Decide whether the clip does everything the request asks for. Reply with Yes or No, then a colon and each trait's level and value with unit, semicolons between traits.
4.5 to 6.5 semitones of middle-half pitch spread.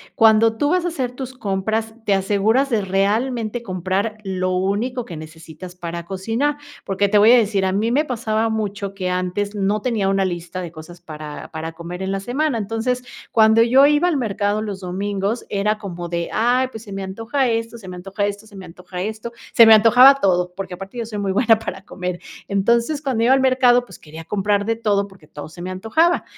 No: average, 3.7 semitones